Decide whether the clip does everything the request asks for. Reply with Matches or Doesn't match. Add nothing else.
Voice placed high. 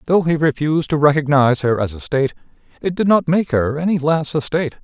Doesn't match